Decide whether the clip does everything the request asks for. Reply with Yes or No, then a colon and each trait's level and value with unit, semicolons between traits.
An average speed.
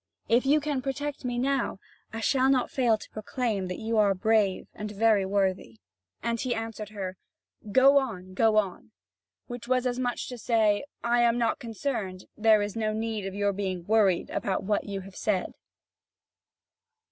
Yes: average, 180 wpm